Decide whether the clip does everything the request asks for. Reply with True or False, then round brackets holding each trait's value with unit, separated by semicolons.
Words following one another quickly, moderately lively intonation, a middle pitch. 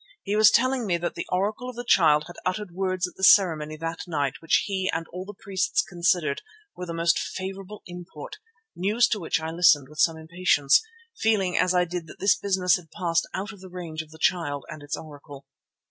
True (220 wpm; 3.1 semitones; 180 Hz)